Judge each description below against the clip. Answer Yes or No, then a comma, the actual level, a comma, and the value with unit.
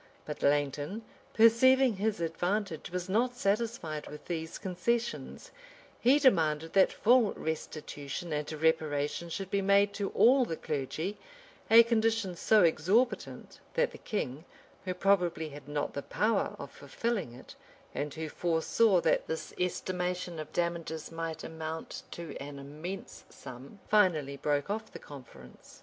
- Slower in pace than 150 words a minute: Yes, average, 140 wpm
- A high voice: No, medium, 170 Hz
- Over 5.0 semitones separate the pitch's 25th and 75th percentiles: Yes, wide, 5.5 semitones